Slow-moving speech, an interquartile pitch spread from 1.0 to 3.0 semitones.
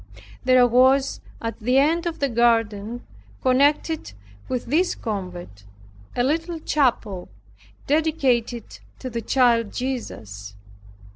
No: slow, 110 wpm; average, 3.7 semitones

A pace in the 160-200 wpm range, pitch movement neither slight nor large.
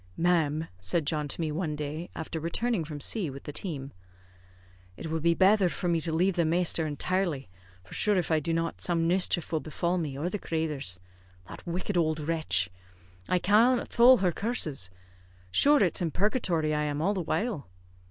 Yes: average, 190 wpm; average, 3.3 semitones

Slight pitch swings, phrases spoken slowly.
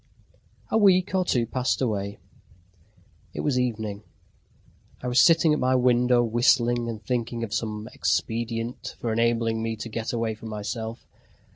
No: narrow, 2.0 semitones; average, 150 wpm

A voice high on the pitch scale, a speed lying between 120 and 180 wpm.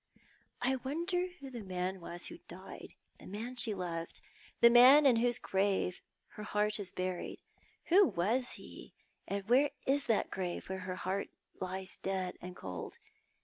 Yes: high, 205 Hz; average, 170 wpm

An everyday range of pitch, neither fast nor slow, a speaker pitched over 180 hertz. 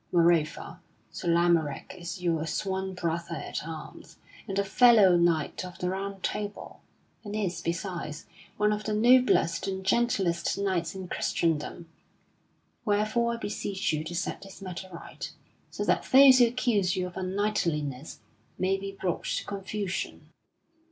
Yes: average, 3.2 semitones; average, 145 wpm; high, 190 Hz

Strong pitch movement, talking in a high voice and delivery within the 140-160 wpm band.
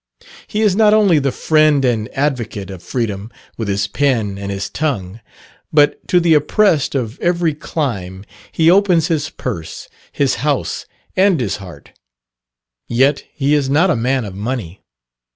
No: wide, 7.3 semitones; low, 135 Hz; average, 155 wpm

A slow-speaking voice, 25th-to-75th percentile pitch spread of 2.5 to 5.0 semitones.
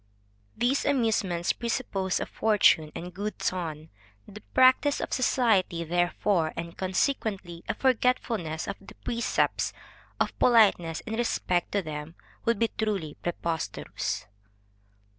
No: slow, 125 wpm; wide, 5.4 semitones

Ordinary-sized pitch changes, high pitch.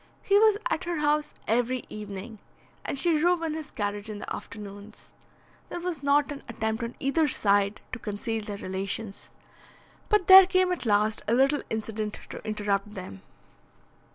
No: wide, 6.6 semitones; high, 225 Hz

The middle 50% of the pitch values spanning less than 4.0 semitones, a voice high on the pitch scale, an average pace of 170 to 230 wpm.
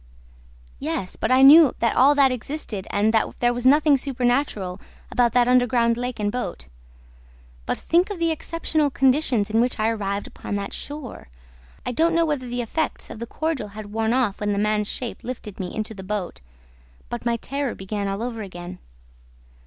No: average, 4.4 semitones; high, 240 Hz; average, 185 wpm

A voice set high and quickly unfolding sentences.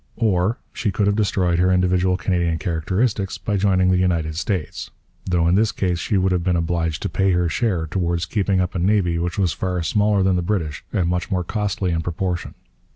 No: very low, 90 Hz; fast, 210 wpm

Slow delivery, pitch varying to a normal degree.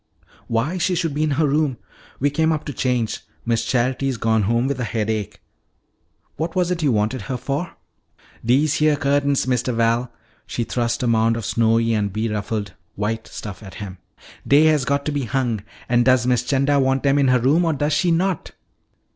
No: average, 195 wpm; average, 4.1 semitones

